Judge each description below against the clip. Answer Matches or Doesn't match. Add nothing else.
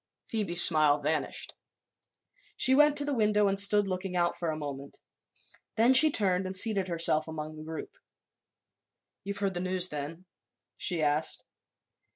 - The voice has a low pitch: Doesn't match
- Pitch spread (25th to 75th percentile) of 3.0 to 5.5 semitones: Matches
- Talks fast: Doesn't match